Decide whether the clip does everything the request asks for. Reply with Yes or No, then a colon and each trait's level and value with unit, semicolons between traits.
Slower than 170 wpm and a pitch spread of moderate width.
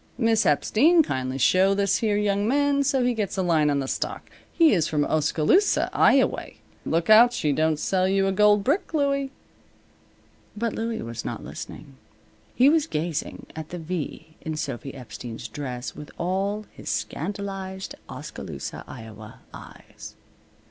No: average, 155 wpm; wide, 6.9 semitones